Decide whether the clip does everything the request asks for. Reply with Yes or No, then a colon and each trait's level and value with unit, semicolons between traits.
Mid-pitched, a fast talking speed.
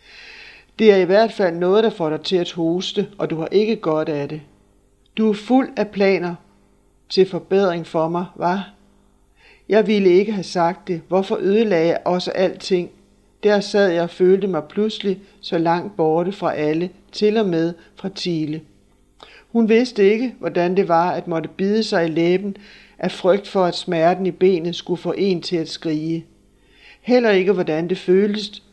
No: medium, 180 Hz; average, 180 wpm